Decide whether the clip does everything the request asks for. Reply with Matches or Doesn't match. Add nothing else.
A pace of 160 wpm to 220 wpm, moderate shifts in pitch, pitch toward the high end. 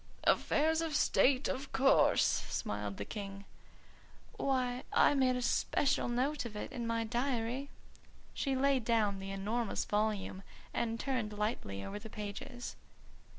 Doesn't match